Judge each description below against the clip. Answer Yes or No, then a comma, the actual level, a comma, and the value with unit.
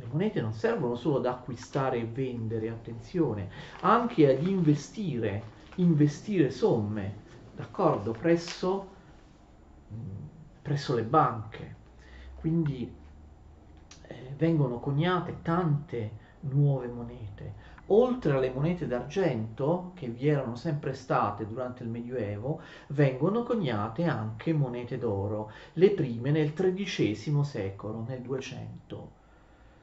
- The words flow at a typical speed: No, slow, 105 wpm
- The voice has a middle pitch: No, low, 130 Hz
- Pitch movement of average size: No, wide, 6.2 semitones